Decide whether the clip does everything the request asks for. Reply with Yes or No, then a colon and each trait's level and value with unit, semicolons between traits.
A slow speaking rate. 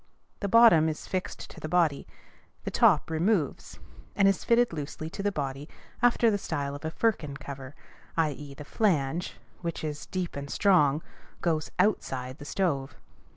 No: average, 160 wpm